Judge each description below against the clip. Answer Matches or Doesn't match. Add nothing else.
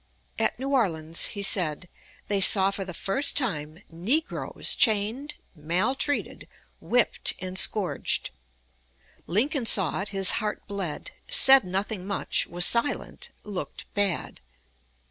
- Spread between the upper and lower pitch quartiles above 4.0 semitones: Matches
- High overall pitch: Matches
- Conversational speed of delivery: Doesn't match